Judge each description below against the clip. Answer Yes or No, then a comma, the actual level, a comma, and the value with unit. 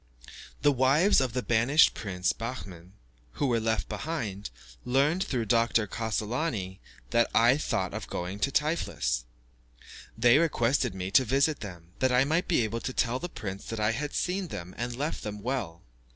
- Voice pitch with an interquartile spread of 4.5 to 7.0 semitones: Yes, average, 4.9 semitones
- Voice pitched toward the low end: Yes, low, 120 Hz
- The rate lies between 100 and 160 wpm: No, average, 170 wpm